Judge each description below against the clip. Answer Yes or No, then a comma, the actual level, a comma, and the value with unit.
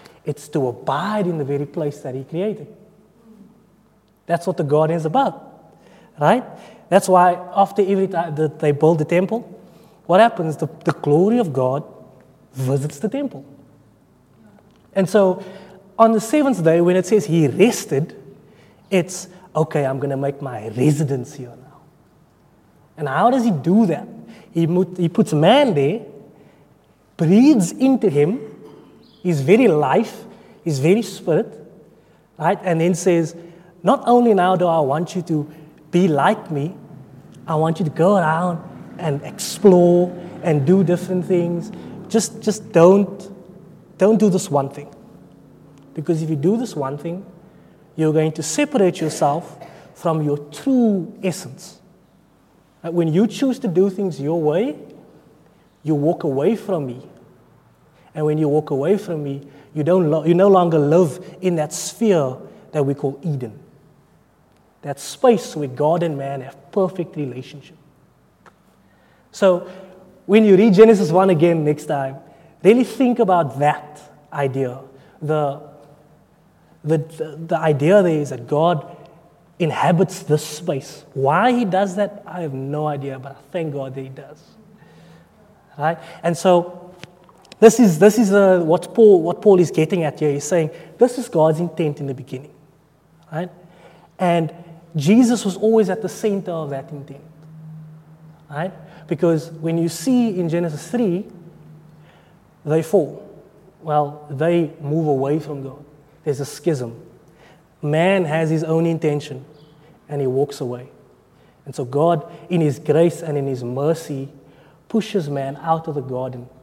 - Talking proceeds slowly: No, average, 150 wpm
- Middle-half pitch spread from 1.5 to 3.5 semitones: No, average, 4.2 semitones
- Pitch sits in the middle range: Yes, medium, 165 Hz